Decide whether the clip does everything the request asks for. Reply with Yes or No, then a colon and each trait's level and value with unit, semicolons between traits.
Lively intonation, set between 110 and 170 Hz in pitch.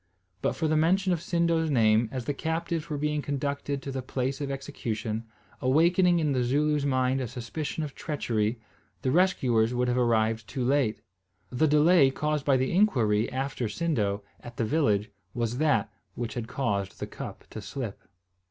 No: average, 4.5 semitones; low, 135 Hz